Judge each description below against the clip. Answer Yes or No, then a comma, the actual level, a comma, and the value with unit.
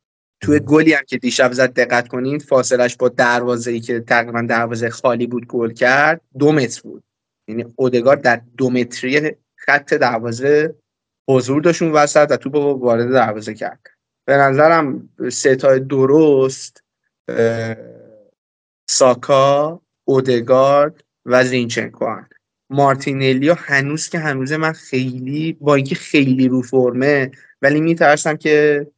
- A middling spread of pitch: Yes, average, 3.2 semitones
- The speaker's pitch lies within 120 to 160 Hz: Yes, low, 130 Hz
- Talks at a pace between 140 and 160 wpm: No, average, 125 wpm